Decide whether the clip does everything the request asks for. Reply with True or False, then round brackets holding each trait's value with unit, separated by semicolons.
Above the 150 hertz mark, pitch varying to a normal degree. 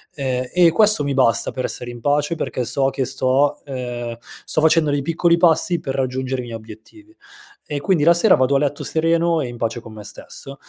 False (140 Hz; 4.6 semitones)